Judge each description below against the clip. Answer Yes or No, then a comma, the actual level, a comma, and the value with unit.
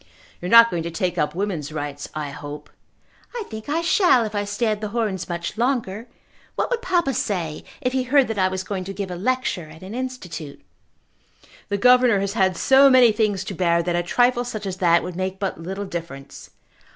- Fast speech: Yes, fast, 215 wpm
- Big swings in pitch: Yes, wide, 5.7 semitones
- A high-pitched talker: Yes, high, 195 Hz